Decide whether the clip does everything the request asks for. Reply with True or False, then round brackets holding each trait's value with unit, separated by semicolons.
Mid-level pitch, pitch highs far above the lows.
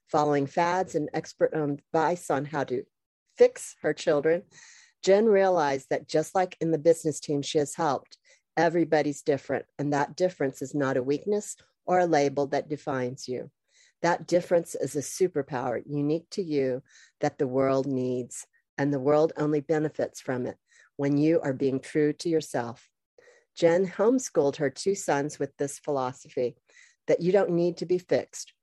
False (155 Hz; 4.2 semitones)